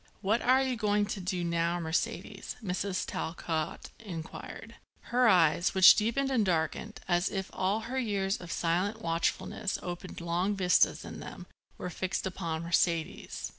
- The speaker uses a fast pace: No, average, 150 wpm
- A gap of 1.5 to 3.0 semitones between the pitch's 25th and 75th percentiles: No, average, 3.8 semitones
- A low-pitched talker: No, medium, 185 Hz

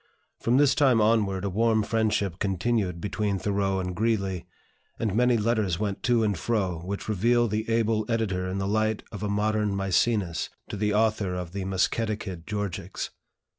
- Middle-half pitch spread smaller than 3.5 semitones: Yes, narrow, 2.6 semitones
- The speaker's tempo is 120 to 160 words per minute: No, average, 170 wpm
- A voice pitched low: Yes, low, 105 Hz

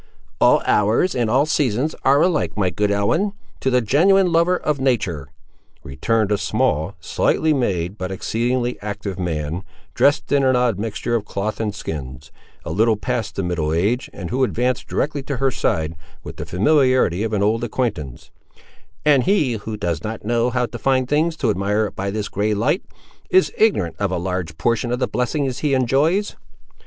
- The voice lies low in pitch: Yes, low, 115 Hz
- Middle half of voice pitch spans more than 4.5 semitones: Yes, average, 5.2 semitones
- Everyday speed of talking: Yes, average, 180 wpm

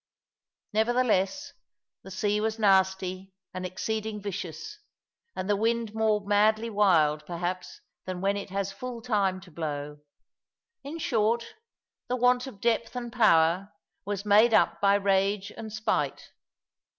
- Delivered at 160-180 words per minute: No, slow, 135 wpm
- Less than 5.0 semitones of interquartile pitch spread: Yes, average, 3.0 semitones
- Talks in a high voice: Yes, high, 205 Hz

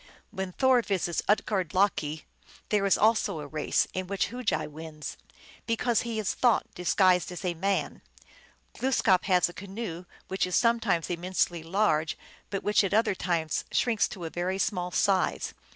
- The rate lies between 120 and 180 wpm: Yes, average, 160 wpm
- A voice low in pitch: No, high, 190 Hz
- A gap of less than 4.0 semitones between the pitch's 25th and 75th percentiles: Yes, average, 3.3 semitones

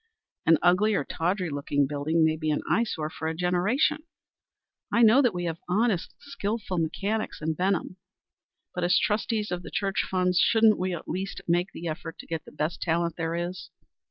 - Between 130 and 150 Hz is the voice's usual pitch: No, medium, 180 Hz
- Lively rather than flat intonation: No, average, 3.9 semitones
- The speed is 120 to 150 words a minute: No, average, 190 wpm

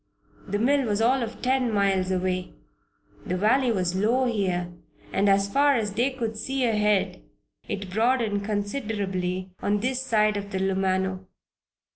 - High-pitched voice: Yes, high, 205 Hz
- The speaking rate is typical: Yes, average, 150 wpm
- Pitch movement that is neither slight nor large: Yes, average, 3.9 semitones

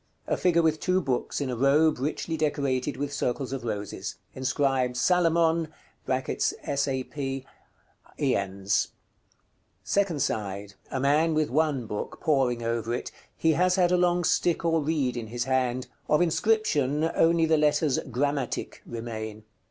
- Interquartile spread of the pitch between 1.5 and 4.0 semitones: No, average, 4.5 semitones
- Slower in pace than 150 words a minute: Yes, average, 140 wpm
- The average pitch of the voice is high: No, medium, 140 Hz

